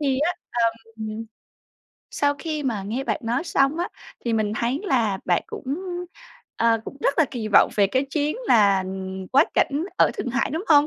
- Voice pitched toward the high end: Yes, very high, 260 Hz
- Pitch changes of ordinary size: Yes, average, 4.5 semitones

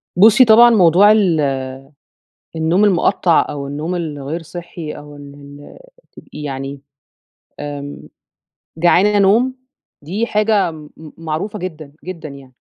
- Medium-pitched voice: Yes, medium, 165 Hz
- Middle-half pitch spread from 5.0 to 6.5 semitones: Yes, wide, 5.5 semitones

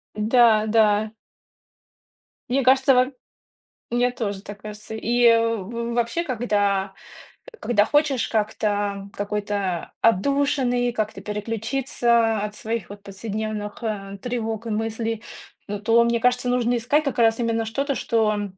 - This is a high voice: Yes, high, 225 Hz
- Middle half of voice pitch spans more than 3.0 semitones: No, average, 2.7 semitones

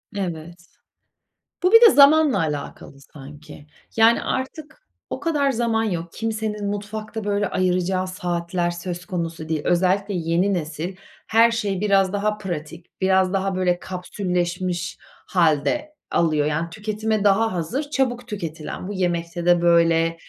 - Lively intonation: No, average, 4.0 semitones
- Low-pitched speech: No, medium, 185 Hz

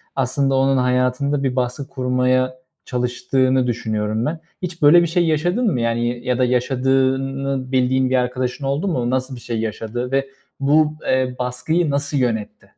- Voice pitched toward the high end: No, low, 130 Hz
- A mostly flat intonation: Yes, narrow, 1.9 semitones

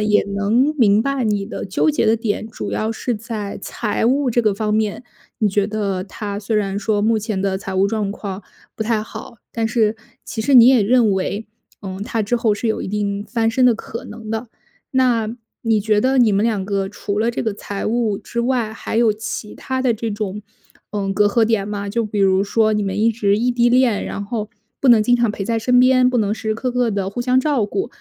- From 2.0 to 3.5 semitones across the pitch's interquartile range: Yes, narrow, 2.5 semitones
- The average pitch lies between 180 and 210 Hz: No, high, 220 Hz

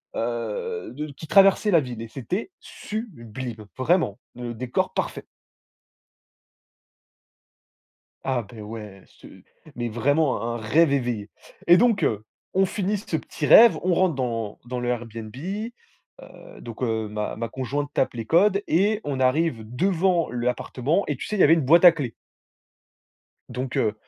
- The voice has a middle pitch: No, low, 130 Hz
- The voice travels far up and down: Yes, wide, 7.2 semitones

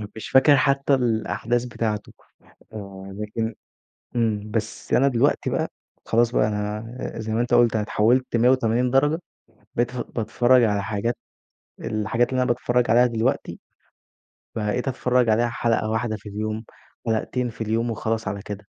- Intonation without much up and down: Yes, narrow, 2.3 semitones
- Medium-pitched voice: No, low, 115 Hz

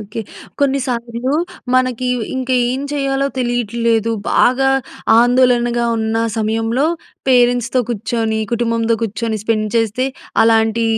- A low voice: No, high, 235 Hz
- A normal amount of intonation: No, narrow, 2.0 semitones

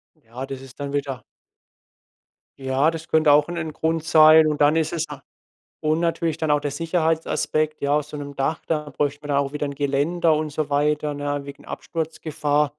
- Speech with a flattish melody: Yes, narrow, 1.8 semitones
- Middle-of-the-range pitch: Yes, medium, 150 Hz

